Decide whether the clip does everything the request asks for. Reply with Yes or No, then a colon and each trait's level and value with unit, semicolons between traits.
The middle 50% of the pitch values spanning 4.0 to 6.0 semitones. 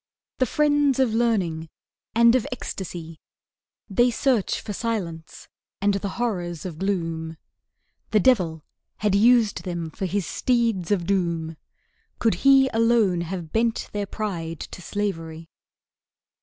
Yes: wide, 5.5 semitones